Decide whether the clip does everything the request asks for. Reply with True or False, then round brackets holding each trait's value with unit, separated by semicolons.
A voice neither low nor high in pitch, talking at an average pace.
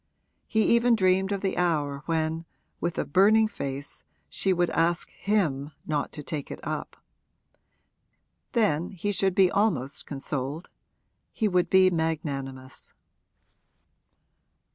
False (170 Hz; 120 wpm)